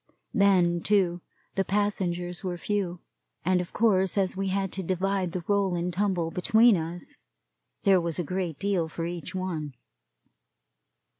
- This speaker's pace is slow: No, average, 150 wpm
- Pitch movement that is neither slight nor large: No, narrow, 2.2 semitones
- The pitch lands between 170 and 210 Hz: Yes, medium, 185 Hz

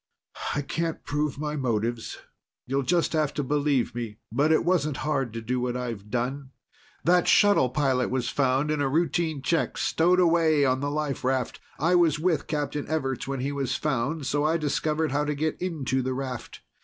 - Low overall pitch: No, medium, 145 Hz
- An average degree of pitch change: Yes, average, 3.2 semitones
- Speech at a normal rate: Yes, average, 190 wpm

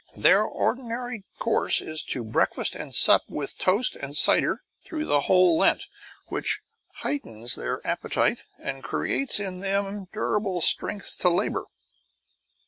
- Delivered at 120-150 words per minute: Yes, slow, 135 wpm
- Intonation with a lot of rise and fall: Yes, wide, 6.1 semitones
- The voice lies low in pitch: No, high, 195 Hz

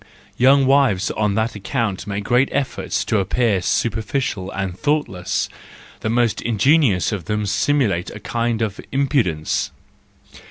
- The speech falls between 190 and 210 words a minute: No, slow, 135 wpm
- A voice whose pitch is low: Yes, low, 110 Hz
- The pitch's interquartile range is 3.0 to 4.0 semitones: No, average, 4.9 semitones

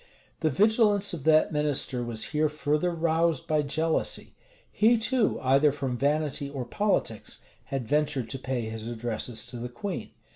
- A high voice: No, medium, 150 Hz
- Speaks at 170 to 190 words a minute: No, average, 155 wpm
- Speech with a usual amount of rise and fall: Yes, average, 4.7 semitones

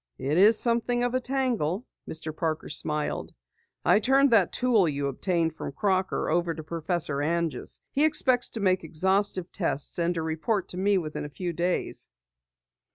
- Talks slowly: No, average, 165 wpm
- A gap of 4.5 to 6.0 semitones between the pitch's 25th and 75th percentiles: Yes, wide, 5.6 semitones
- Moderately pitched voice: Yes, medium, 180 Hz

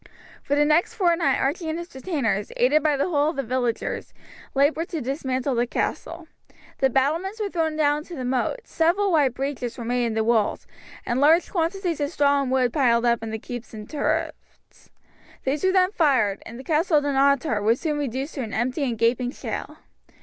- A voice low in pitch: No, very high, 280 Hz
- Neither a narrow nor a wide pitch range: Yes, average, 4.6 semitones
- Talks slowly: No, average, 200 wpm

